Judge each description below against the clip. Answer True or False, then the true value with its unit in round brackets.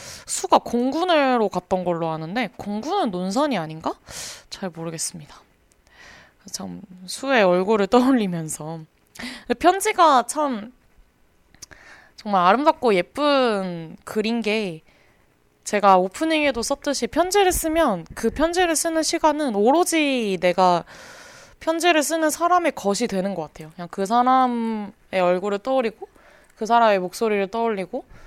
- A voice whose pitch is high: True (225 Hz)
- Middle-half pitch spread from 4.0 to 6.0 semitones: False (8.4 semitones)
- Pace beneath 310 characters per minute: True (265 characters per minute)